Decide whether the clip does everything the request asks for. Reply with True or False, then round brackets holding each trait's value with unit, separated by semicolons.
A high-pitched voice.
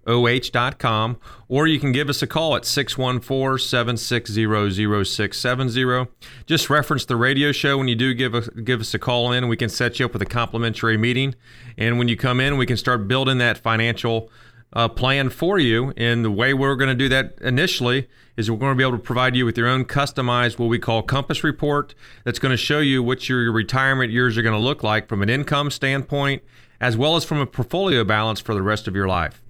False (125 Hz)